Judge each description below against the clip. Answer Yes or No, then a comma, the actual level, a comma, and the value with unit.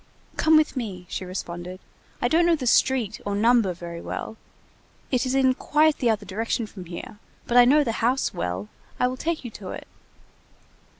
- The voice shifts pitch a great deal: Yes, wide, 5.9 semitones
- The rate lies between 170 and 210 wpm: Yes, average, 190 wpm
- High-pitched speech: Yes, high, 230 Hz